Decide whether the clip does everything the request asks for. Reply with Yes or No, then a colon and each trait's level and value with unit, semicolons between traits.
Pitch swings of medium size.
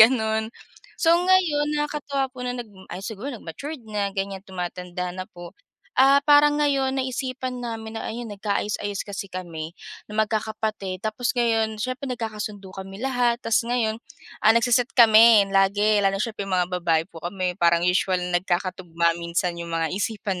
Yes: average, 4.9 semitones